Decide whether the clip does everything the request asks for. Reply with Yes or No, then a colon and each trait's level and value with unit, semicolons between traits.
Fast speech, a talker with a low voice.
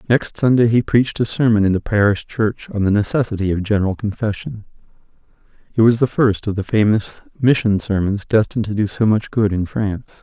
No: average, 195 wpm; low, 105 Hz